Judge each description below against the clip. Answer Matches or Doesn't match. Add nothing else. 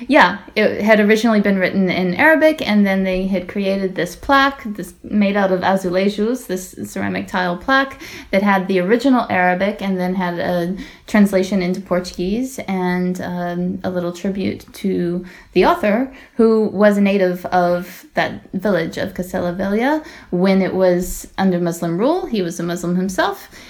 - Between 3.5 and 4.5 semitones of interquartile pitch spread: Doesn't match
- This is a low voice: Doesn't match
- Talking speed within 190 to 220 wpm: Doesn't match